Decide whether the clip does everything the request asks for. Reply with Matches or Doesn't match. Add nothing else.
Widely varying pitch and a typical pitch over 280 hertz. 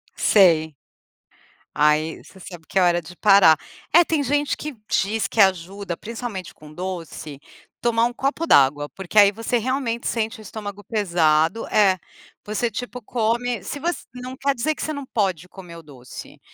Doesn't match